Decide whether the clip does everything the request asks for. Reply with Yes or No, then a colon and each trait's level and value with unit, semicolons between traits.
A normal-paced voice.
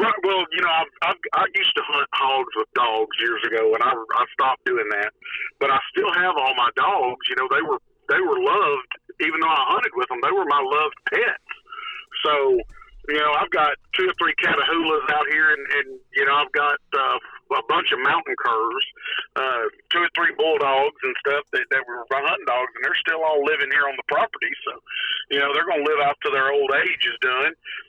No: fast, 225 wpm